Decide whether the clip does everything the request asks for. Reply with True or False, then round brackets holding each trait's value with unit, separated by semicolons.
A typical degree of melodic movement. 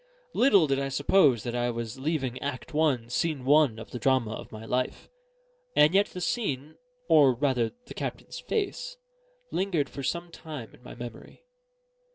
True (4.6 semitones)